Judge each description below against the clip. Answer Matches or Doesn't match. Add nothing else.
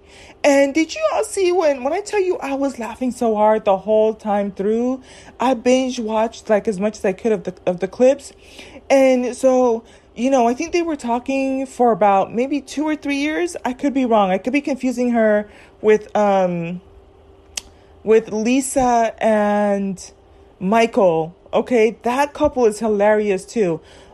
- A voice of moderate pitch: Doesn't match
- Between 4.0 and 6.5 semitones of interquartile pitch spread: Matches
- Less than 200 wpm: Matches